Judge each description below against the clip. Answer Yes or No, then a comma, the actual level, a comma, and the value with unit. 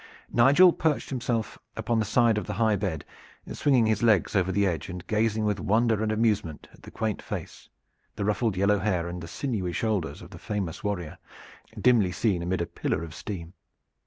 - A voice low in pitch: Yes, low, 105 Hz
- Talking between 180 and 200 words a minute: Yes, average, 190 wpm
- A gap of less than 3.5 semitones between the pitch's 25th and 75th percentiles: No, average, 3.8 semitones